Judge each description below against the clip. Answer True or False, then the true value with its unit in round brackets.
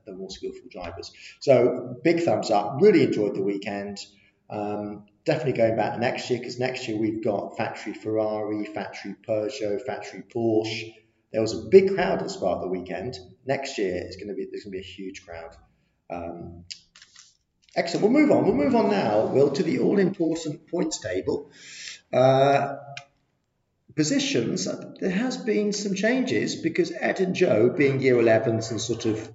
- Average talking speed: True (170 wpm)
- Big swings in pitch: True (6.8 semitones)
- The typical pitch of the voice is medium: False (115 Hz)